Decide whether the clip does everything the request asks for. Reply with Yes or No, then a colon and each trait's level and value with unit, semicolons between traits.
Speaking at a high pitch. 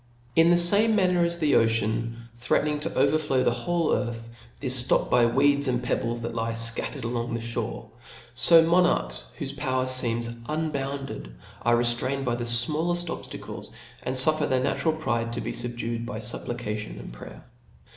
No: low, 125 Hz